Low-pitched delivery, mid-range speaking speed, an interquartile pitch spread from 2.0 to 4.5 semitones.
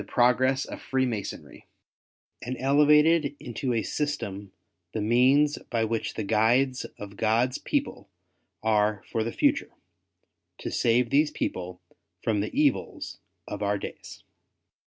No: low, 120 Hz; slow, 125 wpm; average, 4.2 semitones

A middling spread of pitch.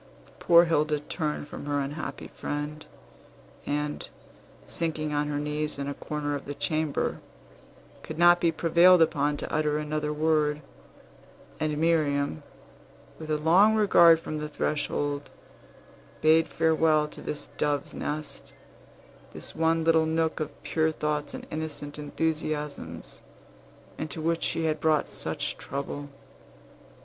No: narrow, 1.6 semitones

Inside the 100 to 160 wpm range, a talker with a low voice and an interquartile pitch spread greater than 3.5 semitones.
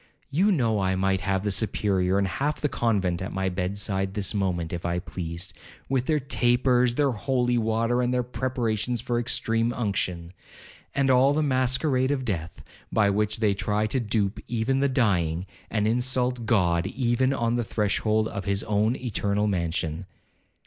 No: average, 170 wpm; low, 110 Hz; average, 4.5 semitones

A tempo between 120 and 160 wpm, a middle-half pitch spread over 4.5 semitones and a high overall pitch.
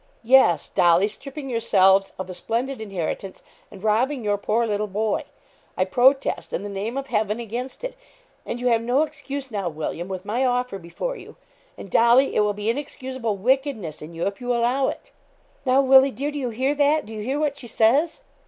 No: average, 200 wpm; average, 4.9 semitones; high, 235 Hz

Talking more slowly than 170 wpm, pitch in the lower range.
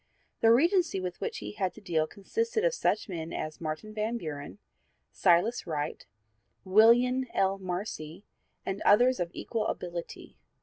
No: average, 145 wpm; high, 195 Hz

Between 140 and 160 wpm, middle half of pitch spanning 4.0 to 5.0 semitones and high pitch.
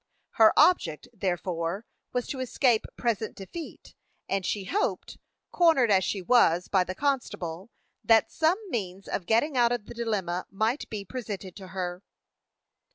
Yes: average, 150 wpm; average, 4.7 semitones; high, 210 Hz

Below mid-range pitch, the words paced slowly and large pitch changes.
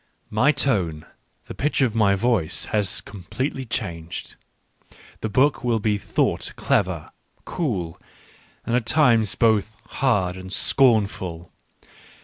No: low, 110 Hz; slow, 120 wpm; average, 5.0 semitones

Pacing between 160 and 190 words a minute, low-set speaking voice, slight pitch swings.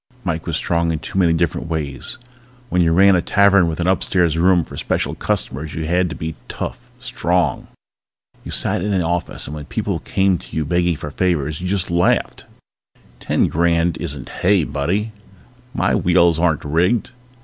Yes: average, 180 wpm; very low, 85 Hz; narrow, 2.3 semitones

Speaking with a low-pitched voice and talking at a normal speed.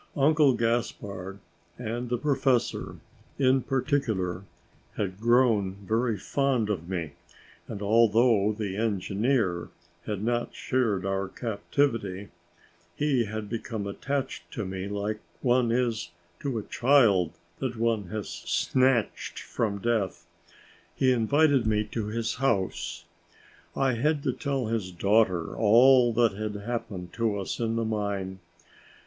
No: low, 110 Hz; slow, 125 wpm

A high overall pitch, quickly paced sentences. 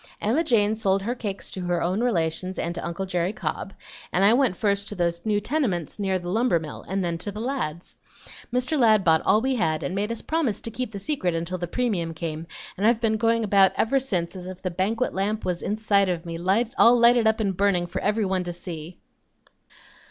Yes: high, 195 Hz; fast, 220 wpm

